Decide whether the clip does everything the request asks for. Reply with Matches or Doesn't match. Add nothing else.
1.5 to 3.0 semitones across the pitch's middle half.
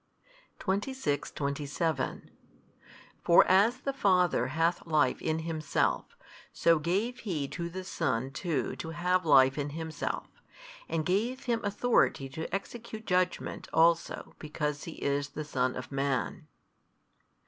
Doesn't match